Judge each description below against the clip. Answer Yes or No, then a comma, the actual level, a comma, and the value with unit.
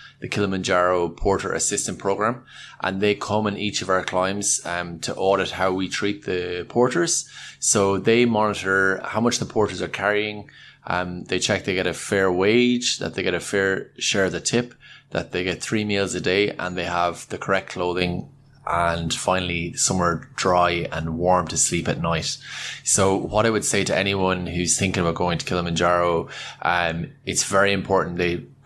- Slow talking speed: No, average, 185 wpm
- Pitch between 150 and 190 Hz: No, very low, 95 Hz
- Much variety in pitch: No, average, 2.7 semitones